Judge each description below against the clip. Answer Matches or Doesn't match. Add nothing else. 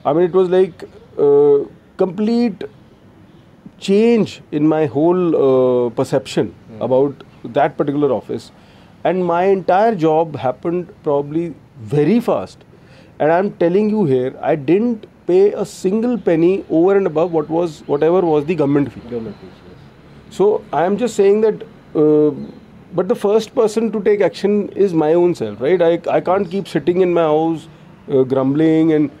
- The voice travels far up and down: Doesn't match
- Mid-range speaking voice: Matches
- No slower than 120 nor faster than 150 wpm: Doesn't match